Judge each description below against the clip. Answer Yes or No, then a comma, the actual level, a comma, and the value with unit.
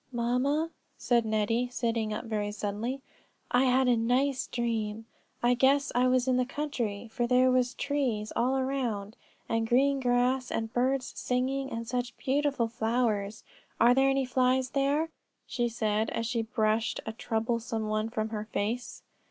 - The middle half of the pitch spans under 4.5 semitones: Yes, average, 2.7 semitones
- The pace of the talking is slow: No, average, 160 wpm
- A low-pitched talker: No, high, 245 Hz